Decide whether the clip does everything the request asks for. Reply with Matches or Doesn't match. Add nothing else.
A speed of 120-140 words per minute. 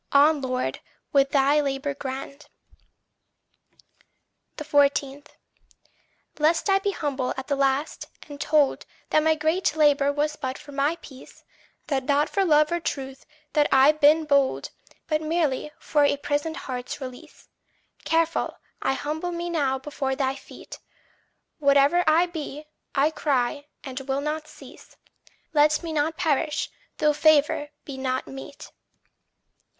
Matches